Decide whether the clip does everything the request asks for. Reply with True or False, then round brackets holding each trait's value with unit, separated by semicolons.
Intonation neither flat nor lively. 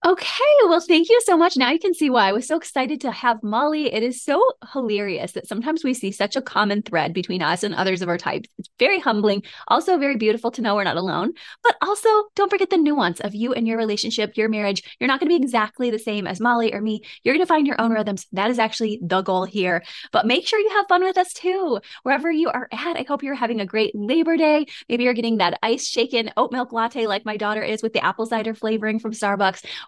False (6.6 semitones)